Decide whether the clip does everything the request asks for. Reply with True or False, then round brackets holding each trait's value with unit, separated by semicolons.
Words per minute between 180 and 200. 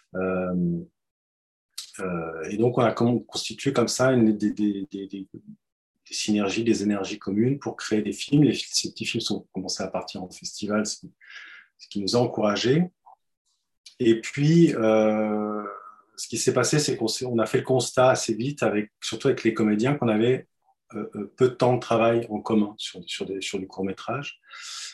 True (185 wpm)